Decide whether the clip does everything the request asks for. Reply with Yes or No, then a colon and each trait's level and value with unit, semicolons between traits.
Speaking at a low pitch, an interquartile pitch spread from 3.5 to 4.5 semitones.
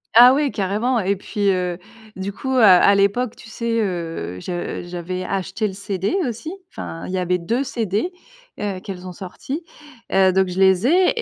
No: high, 195 Hz; average, 4.0 semitones